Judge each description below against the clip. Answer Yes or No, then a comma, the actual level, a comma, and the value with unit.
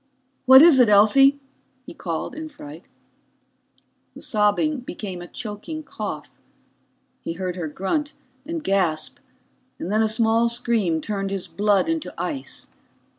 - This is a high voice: Yes, high, 220 Hz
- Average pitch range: No, wide, 6.6 semitones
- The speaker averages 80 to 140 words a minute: Yes, slow, 135 wpm